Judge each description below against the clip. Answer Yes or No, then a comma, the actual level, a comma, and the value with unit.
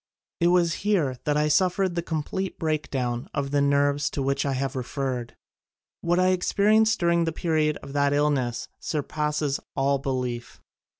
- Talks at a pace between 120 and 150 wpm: No, average, 160 wpm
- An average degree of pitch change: Yes, average, 3.8 semitones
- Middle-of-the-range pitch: Yes, medium, 150 Hz